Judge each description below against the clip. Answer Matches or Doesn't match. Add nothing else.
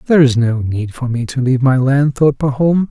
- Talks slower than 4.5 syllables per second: Doesn't match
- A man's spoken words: Matches